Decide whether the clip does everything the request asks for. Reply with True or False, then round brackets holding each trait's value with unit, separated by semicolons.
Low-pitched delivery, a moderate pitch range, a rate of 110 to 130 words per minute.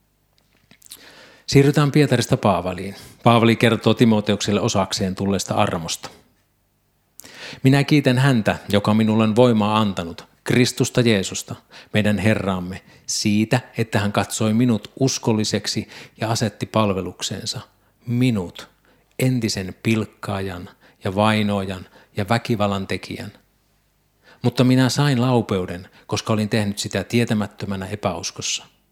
False (110 Hz; 3.4 semitones; 100 wpm)